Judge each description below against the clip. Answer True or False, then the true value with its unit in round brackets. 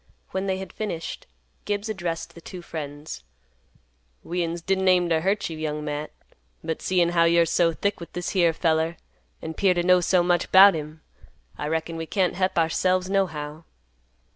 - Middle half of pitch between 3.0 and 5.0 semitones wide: False (2.5 semitones)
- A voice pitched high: False (170 Hz)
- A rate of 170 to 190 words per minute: True (175 wpm)